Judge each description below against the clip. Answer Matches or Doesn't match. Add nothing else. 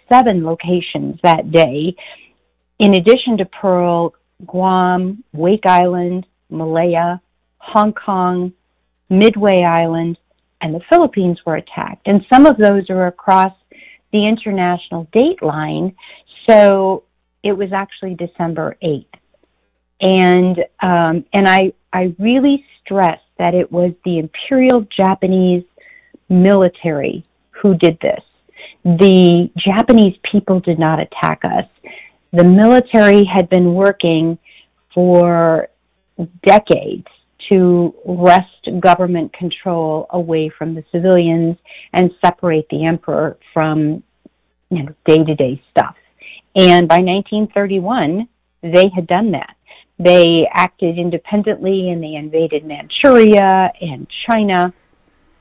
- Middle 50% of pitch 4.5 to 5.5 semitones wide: Doesn't match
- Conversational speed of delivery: Doesn't match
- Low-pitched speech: Doesn't match